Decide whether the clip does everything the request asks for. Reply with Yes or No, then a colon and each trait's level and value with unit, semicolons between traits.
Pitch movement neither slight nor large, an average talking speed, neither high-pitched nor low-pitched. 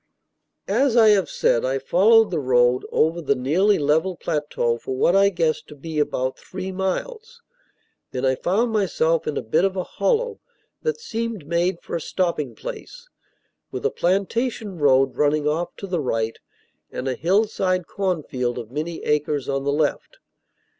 No: wide, 5.9 semitones; average, 165 wpm; medium, 170 Hz